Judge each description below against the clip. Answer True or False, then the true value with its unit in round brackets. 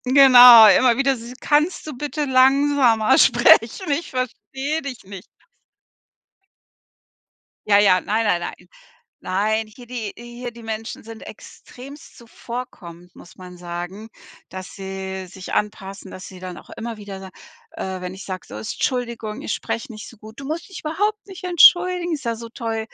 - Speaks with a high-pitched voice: True (230 Hz)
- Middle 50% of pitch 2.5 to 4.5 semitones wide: False (5.5 semitones)